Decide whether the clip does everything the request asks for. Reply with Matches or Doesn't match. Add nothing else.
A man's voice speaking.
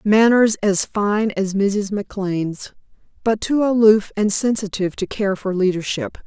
Doesn't match